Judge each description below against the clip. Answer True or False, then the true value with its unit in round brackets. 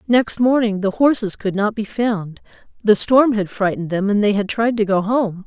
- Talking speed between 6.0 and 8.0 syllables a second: False (4.9 syllables/s)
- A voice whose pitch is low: False (210 Hz)